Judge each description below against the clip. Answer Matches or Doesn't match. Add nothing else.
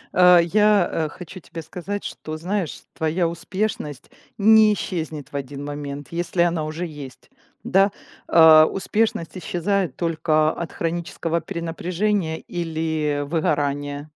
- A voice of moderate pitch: Matches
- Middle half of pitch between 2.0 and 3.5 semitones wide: Matches